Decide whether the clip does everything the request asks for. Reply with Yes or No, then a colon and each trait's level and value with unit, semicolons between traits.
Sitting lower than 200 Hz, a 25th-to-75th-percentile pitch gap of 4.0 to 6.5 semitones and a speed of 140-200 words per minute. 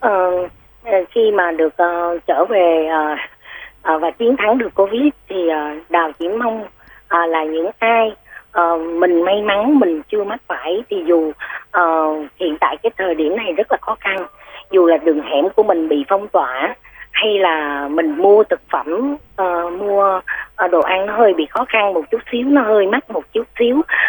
Yes: high, 190 Hz; average, 5.2 semitones; average, 195 wpm